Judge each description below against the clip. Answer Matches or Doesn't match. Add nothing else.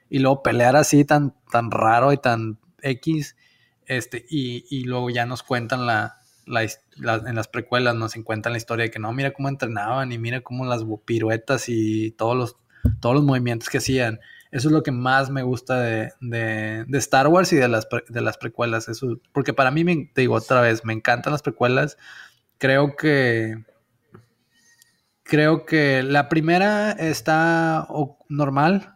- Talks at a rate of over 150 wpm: Matches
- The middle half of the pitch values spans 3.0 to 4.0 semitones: Matches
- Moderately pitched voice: Doesn't match